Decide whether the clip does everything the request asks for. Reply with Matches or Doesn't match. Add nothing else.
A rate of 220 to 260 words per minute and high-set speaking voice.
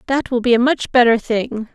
Matches